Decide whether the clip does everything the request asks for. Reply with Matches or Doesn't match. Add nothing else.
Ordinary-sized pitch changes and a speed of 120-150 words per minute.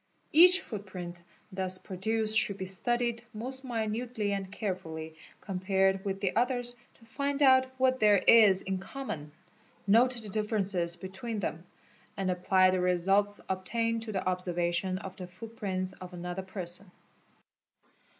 Matches